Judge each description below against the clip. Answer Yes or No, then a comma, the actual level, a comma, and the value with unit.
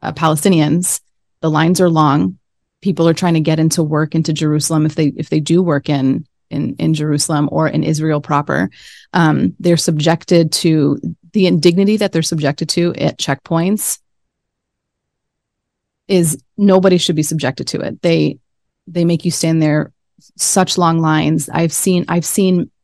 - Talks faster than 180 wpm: No, average, 160 wpm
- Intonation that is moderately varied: No, narrow, 2.2 semitones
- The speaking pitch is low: No, medium, 165 Hz